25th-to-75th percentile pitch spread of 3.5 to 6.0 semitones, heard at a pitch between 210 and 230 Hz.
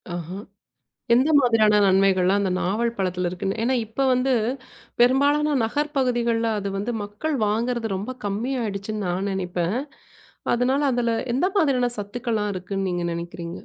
Yes: average, 4.5 semitones; high, 220 Hz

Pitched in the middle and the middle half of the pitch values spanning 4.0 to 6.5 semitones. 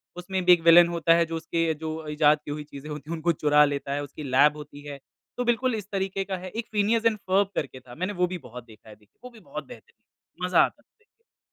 Yes: medium, 165 Hz; average, 4.7 semitones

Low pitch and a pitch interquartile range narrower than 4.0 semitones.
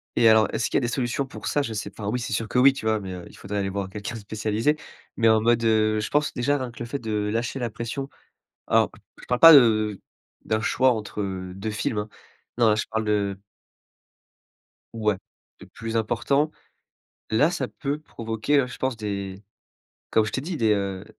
Yes: low, 110 Hz; average, 2.9 semitones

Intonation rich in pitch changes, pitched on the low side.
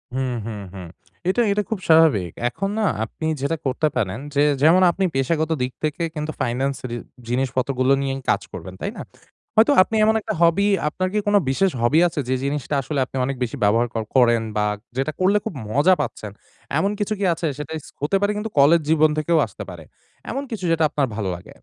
No: wide, 6.2 semitones; medium, 150 Hz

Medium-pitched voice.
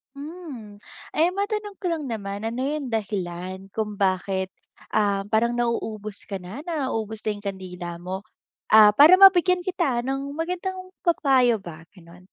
No: high, 225 Hz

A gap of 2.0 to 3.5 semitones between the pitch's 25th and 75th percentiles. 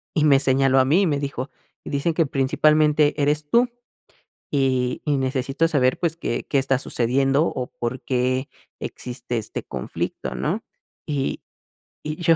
Yes: average, 2.8 semitones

